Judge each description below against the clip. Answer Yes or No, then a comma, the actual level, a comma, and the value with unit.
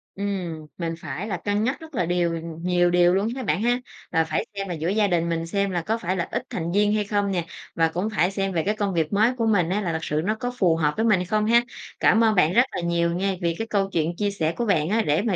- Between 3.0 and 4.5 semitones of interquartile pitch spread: Yes, average, 3.7 semitones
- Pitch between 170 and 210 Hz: Yes, high, 190 Hz